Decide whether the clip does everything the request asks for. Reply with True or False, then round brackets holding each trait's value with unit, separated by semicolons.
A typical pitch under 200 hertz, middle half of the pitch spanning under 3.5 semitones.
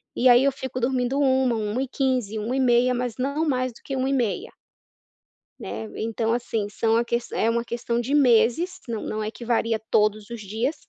False (240 Hz; 2.7 semitones)